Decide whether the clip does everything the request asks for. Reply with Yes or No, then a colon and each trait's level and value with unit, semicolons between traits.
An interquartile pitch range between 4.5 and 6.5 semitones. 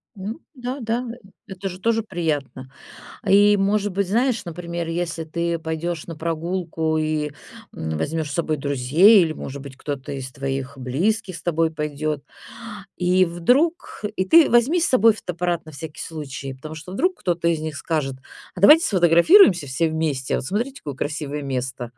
Yes: average, 4.8 semitones